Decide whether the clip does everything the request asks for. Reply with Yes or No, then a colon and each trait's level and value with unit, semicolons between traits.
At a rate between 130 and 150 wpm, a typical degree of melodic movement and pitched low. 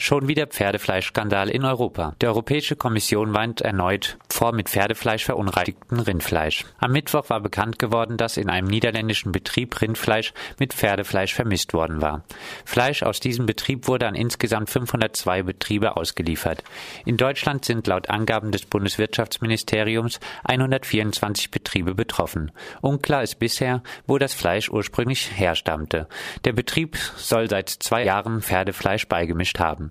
Yes: average, 135 wpm; average, 3.8 semitones; low, 110 Hz